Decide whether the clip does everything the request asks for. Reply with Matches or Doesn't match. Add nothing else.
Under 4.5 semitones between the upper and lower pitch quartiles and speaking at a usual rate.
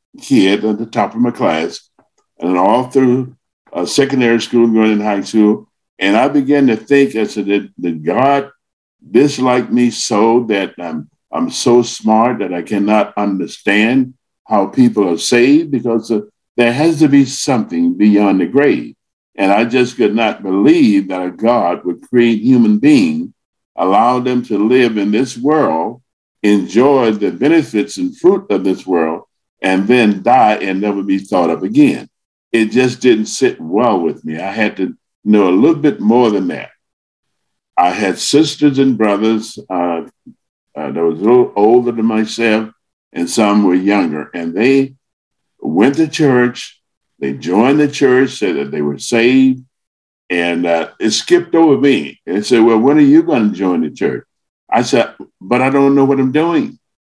Doesn't match